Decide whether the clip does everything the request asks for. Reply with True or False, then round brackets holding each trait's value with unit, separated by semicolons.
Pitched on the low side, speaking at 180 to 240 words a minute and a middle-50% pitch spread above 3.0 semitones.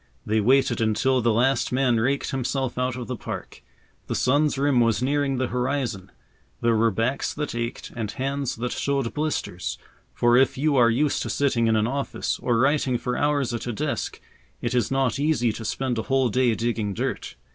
False (125 Hz; 195 wpm; 2.7 semitones)